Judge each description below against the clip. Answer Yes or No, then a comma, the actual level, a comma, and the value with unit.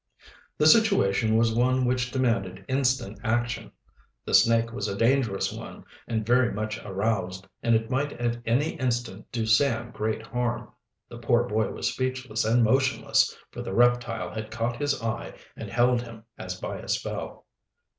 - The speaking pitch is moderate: No, low, 120 Hz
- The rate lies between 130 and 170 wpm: Yes, average, 165 wpm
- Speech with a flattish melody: Yes, narrow, 2.3 semitones